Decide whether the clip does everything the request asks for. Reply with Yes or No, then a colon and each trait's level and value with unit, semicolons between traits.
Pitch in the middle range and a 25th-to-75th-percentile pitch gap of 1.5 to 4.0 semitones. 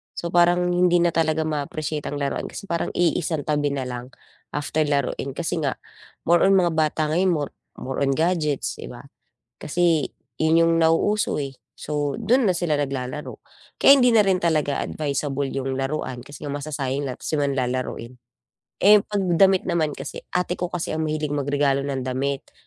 Yes: medium, 150 Hz; average, 3.6 semitones